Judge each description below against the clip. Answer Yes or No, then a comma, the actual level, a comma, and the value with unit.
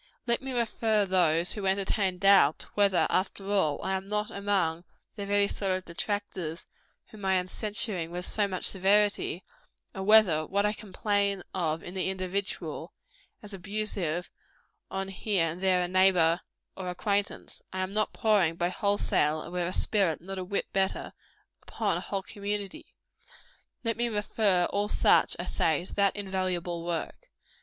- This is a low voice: No, high, 190 Hz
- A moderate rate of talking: Yes, average, 165 wpm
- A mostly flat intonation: Yes, narrow, 2.3 semitones